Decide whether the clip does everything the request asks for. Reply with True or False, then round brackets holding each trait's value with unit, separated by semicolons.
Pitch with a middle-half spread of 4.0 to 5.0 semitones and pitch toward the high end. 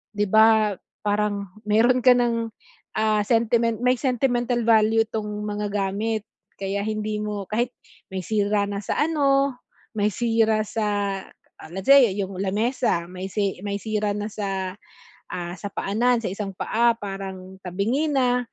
False (2.7 semitones; 215 Hz)